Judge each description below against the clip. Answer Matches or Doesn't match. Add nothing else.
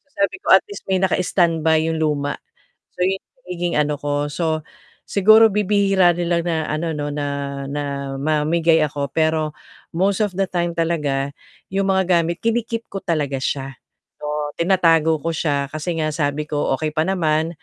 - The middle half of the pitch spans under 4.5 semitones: Matches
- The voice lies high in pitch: Doesn't match